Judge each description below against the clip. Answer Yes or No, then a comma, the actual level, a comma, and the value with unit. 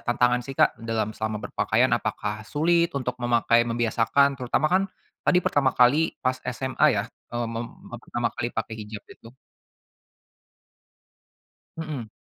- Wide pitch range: No, average, 3.1 semitones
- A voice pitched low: Yes, low, 120 Hz